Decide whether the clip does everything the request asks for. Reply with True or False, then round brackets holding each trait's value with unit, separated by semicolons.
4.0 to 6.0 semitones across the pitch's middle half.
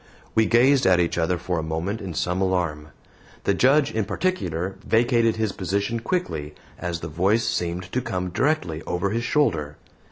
True (5.4 semitones)